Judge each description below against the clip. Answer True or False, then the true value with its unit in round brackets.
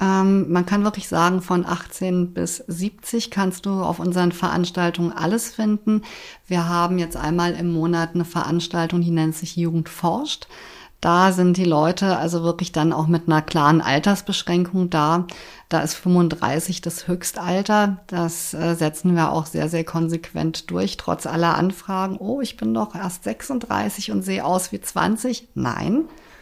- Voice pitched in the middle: True (175 Hz)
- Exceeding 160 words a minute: False (155 wpm)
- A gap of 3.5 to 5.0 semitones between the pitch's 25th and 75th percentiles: False (2.5 semitones)